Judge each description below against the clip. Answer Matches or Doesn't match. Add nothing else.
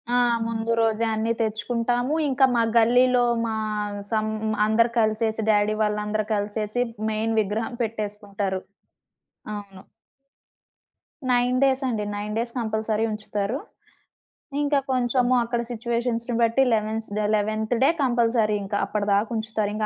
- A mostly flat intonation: Matches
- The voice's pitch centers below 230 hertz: Matches